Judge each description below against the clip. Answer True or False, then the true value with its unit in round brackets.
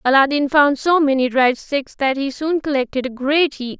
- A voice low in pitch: False (275 Hz)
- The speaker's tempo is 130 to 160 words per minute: False (205 wpm)